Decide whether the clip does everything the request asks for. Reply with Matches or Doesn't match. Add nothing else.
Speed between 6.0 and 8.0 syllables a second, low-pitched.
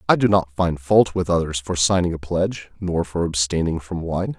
Doesn't match